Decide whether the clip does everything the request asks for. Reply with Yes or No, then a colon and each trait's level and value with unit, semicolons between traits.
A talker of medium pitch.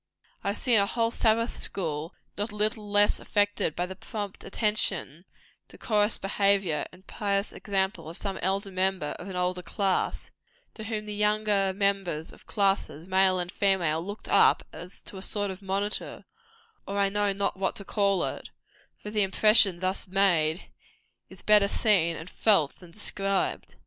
No: high, 195 Hz